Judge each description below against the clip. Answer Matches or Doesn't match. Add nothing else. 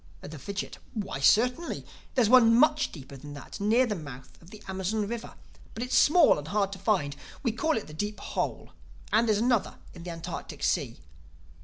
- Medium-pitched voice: Doesn't match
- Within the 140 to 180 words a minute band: Doesn't match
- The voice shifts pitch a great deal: Matches